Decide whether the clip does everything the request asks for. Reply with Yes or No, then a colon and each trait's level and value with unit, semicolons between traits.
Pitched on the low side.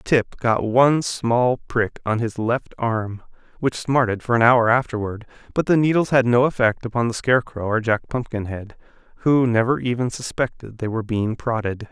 Yes: low, 120 Hz